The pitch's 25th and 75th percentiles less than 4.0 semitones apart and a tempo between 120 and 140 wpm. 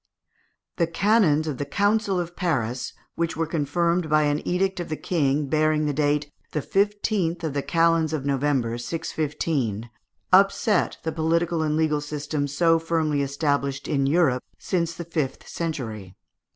No: average, 2.9 semitones; average, 150 wpm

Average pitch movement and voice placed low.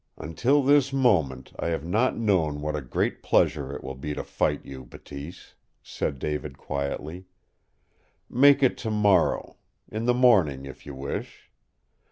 No: wide, 8.6 semitones; very low, 80 Hz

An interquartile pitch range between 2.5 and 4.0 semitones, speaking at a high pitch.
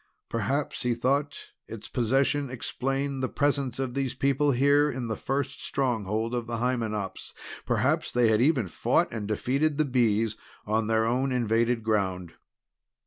No: average, 3.5 semitones; low, 125 Hz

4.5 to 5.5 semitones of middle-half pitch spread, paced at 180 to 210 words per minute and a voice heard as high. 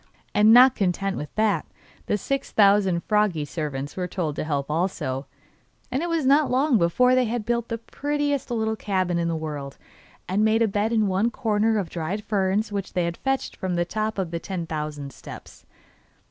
Yes: average, 4.9 semitones; average, 190 wpm; high, 200 Hz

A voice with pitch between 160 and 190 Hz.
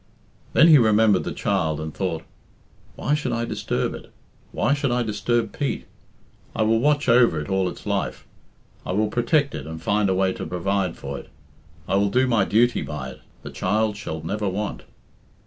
No: low, 105 Hz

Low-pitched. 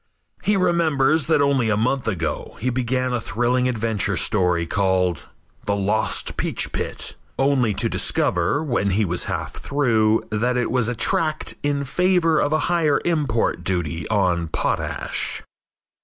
Yes: low, 120 Hz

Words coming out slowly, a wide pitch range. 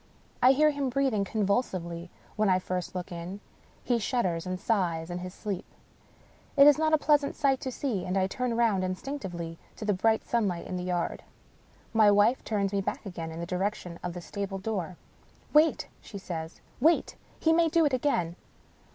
No: average, 195 wpm; wide, 5.9 semitones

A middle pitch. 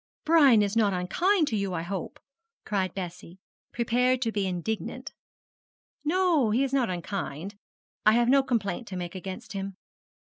No: high, 210 Hz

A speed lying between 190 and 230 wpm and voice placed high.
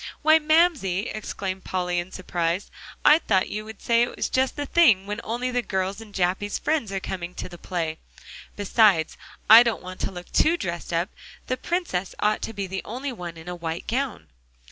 Yes: average, 195 wpm; high, 200 Hz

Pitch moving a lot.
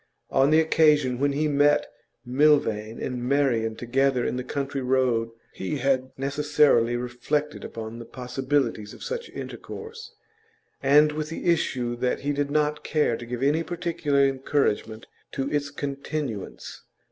No: average, 3.3 semitones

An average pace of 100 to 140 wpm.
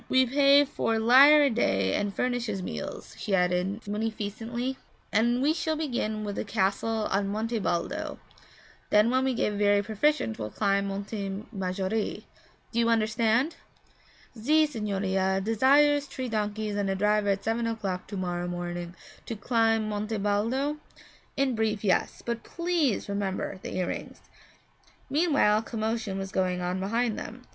No: average, 150 wpm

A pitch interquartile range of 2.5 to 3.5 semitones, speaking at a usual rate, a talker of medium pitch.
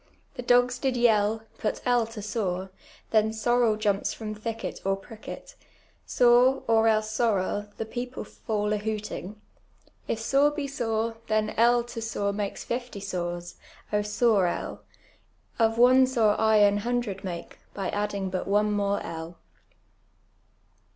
No: average, 2.8 semitones; average, 145 wpm; high, 220 Hz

